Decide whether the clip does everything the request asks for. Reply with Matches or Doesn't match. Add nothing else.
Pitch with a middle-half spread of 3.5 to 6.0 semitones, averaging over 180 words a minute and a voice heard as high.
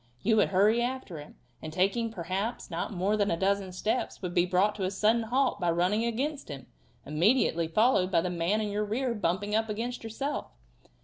Matches